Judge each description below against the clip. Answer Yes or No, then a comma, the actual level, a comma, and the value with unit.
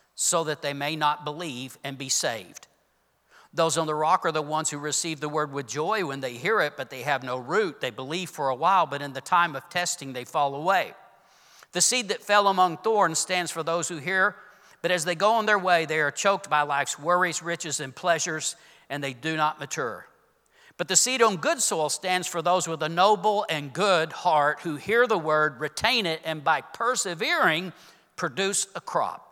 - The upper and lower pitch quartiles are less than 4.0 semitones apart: Yes, average, 3.5 semitones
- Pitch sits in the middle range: Yes, medium, 165 Hz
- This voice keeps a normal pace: No, fast, 215 wpm